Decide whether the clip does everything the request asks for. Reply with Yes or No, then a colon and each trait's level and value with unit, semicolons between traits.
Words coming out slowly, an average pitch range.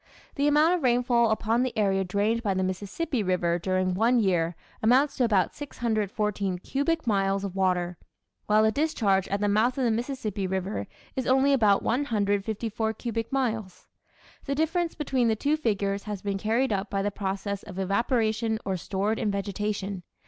No: average, 170 wpm; average, 4.0 semitones